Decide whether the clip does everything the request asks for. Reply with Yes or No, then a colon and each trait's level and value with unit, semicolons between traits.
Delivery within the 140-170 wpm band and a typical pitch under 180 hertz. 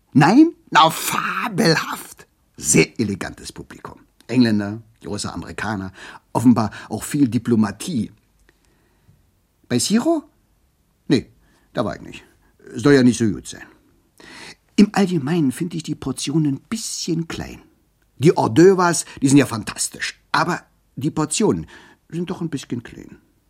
No: average, 130 wpm; medium, 140 Hz